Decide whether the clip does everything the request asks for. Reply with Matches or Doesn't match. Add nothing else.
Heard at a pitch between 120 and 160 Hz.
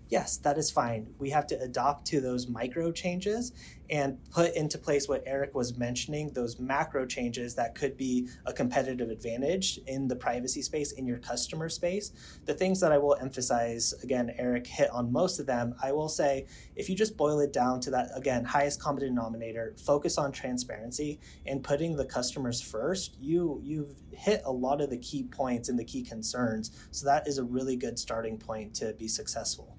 Matches